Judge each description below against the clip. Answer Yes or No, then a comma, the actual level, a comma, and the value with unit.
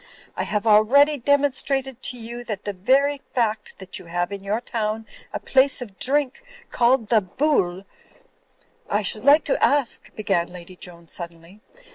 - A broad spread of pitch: Yes, wide, 5.7 semitones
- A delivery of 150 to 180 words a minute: Yes, average, 160 wpm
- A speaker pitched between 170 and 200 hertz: No, high, 220 Hz